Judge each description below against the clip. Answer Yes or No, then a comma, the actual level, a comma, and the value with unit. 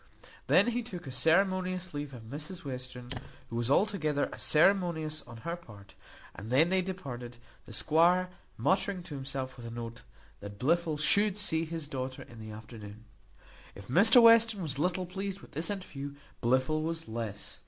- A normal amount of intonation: No, wide, 6.7 semitones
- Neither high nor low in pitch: Yes, medium, 155 Hz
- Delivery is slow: No, average, 170 wpm